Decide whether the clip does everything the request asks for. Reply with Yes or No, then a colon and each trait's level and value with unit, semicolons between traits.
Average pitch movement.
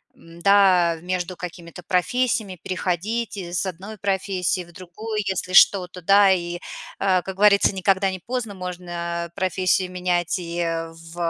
No: narrow, 2.1 semitones